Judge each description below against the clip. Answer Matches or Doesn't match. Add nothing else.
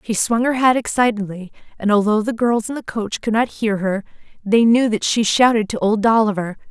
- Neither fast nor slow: Doesn't match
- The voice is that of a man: Doesn't match